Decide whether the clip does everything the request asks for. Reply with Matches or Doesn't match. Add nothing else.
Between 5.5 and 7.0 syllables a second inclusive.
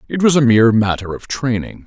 Matches